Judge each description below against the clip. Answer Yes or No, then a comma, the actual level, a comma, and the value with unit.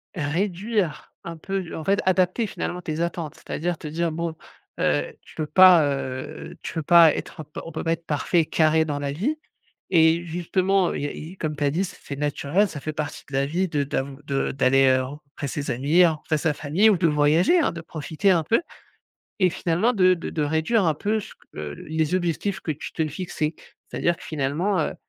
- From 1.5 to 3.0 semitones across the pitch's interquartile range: No, average, 3.5 semitones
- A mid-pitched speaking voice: Yes, medium, 160 Hz